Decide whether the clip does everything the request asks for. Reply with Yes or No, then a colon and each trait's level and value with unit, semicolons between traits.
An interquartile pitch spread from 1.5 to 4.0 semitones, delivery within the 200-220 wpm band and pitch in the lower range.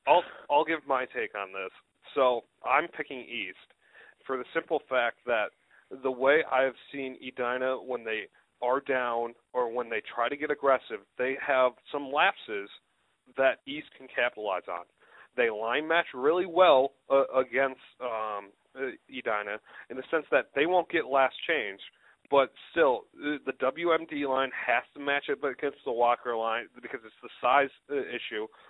No: average, 2.9 semitones; average, 165 wpm; low, 130 Hz